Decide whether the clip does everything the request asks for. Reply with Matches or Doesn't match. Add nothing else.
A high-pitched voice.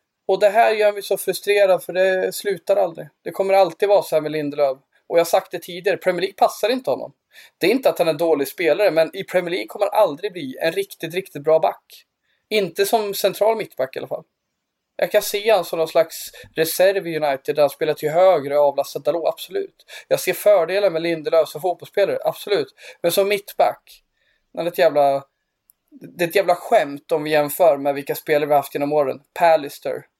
Doesn't match